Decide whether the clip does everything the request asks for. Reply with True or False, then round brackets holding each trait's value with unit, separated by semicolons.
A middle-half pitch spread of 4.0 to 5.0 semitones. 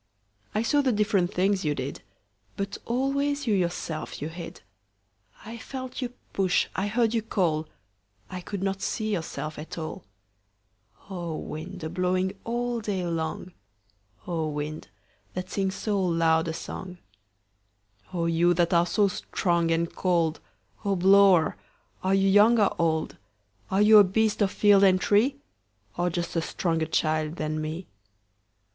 True (4.4 semitones)